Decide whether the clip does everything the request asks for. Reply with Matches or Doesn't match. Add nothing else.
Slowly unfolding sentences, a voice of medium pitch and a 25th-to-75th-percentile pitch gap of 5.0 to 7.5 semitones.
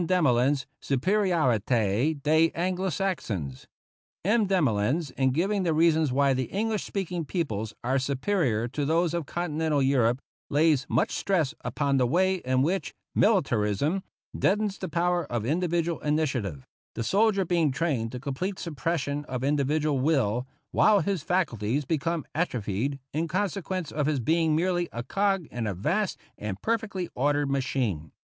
Doesn't match